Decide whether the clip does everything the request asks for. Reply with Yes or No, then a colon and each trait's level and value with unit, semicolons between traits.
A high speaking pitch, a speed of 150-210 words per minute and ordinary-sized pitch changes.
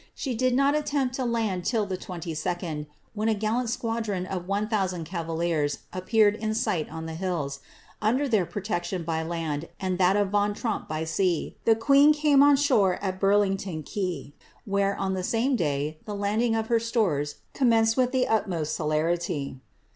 Yes: high, 195 Hz; average, 175 wpm; average, 5.0 semitones